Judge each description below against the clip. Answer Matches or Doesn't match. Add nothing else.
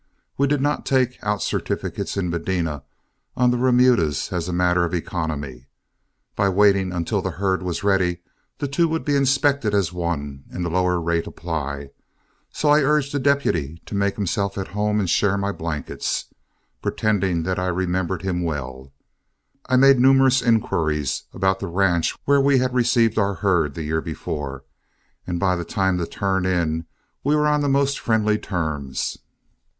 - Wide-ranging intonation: Matches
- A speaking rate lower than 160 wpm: Doesn't match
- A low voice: Matches